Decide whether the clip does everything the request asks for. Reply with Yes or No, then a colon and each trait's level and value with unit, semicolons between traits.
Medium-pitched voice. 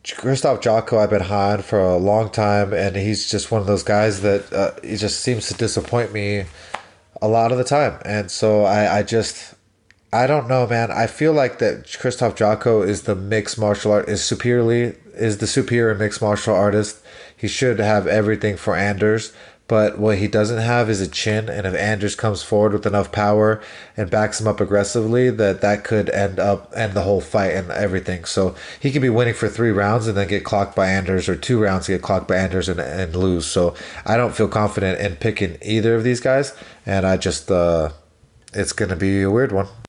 No: low, 105 Hz